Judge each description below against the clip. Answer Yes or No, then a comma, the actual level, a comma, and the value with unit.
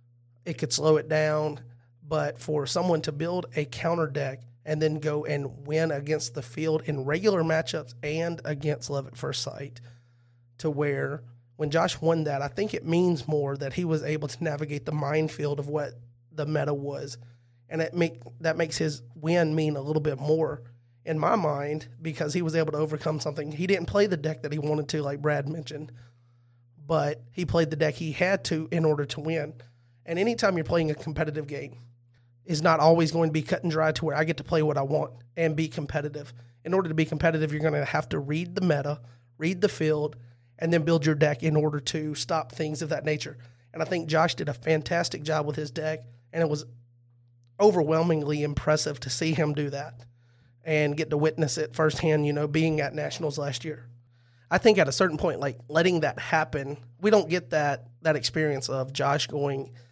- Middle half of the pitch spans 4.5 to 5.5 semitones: No, narrow, 2.5 semitones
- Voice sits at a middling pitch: Yes, medium, 150 Hz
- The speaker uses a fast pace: Yes, fast, 210 wpm